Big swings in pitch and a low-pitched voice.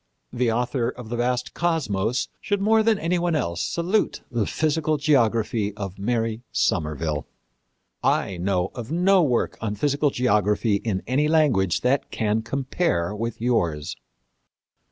Yes: wide, 6.5 semitones; low, 120 Hz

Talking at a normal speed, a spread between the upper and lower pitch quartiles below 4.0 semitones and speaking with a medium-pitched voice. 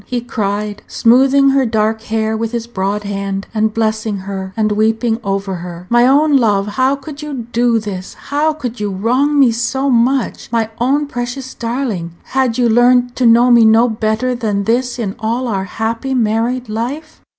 No: average, 180 wpm; average, 3.1 semitones; high, 230 Hz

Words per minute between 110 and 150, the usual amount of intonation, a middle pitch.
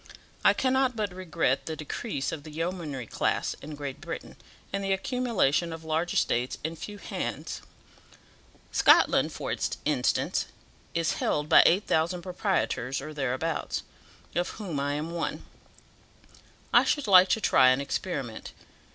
Yes: average, 140 wpm; average, 4.8 semitones; medium, 165 Hz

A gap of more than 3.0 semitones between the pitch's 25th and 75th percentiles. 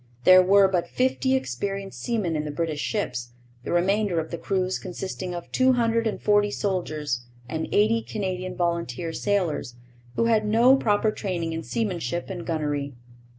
Yes: average, 4.3 semitones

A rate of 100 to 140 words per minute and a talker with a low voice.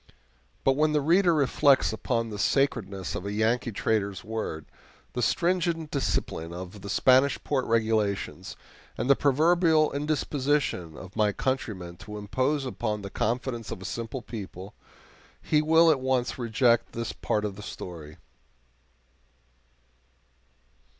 Yes: slow, 135 wpm; low, 120 Hz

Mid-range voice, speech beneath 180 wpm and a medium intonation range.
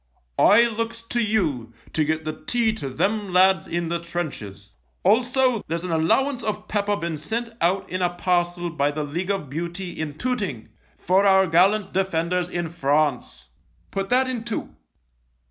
Yes: medium, 180 Hz; average, 170 wpm; average, 5.0 semitones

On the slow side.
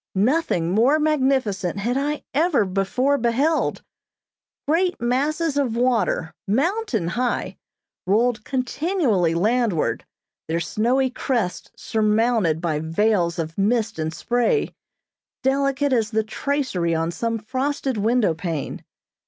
Yes: slow, 110 wpm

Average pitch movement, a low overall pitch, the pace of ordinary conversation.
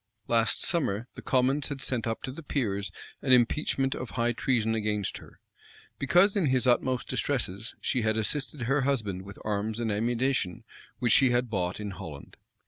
Yes: average, 3.9 semitones; low, 120 Hz; average, 175 wpm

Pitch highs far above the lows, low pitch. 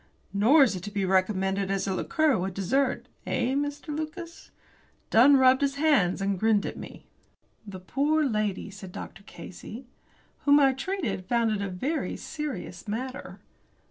No: wide, 6.6 semitones; high, 230 Hz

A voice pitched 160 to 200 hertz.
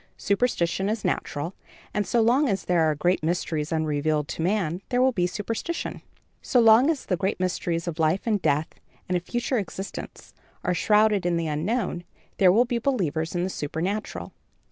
Yes: medium, 185 Hz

